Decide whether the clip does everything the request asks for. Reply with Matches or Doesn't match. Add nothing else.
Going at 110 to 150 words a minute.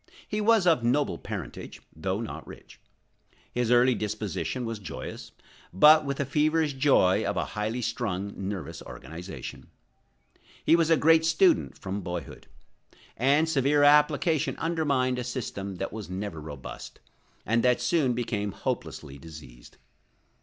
Matches